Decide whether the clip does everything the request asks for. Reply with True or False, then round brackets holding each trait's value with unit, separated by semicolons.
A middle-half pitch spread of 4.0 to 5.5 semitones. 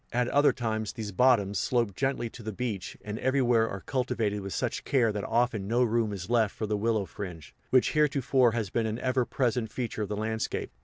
False (3.1 semitones)